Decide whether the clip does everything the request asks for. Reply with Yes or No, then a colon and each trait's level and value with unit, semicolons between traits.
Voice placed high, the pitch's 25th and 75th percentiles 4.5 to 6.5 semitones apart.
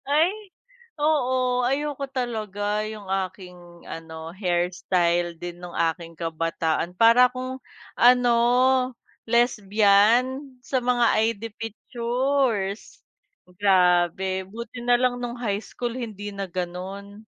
Yes: high, 210 Hz; wide, 5.4 semitones